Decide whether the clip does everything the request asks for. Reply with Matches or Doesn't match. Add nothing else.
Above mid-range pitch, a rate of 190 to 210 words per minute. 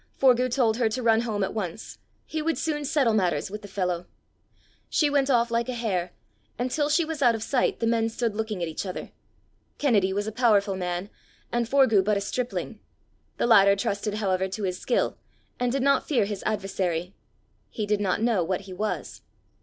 Matches